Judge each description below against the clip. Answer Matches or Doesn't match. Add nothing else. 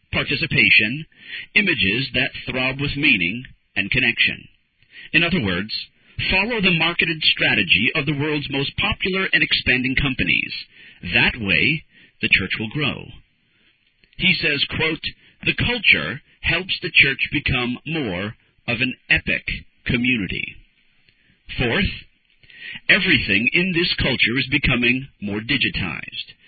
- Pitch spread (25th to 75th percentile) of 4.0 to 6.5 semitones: Matches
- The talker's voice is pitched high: Doesn't match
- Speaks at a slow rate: Matches